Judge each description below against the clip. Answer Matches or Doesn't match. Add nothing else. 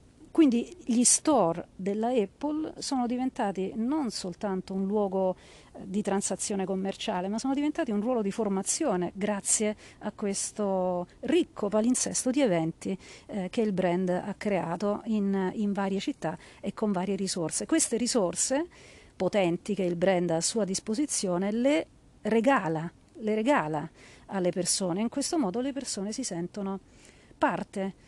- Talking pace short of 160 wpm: Matches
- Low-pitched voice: Doesn't match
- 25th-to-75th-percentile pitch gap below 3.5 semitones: Doesn't match